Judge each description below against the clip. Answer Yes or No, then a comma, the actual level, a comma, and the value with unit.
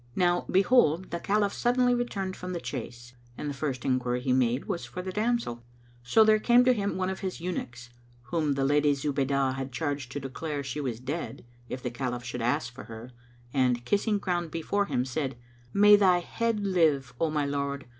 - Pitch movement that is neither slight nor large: No, wide, 6.7 semitones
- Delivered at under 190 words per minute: No, average, 195 wpm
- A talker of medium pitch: Yes, medium, 150 Hz